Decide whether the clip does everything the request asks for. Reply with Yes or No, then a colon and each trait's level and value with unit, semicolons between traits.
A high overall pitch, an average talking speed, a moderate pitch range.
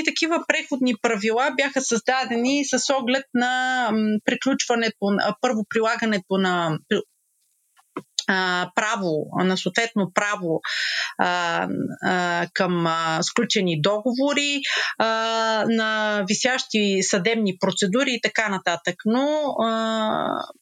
No: high, 225 Hz; slow, 80 wpm; average, 4.9 semitones